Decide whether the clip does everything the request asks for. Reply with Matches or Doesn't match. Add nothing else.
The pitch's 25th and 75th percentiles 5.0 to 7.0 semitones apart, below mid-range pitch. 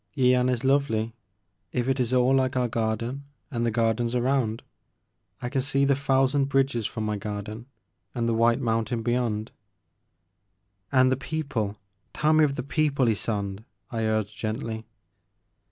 Doesn't match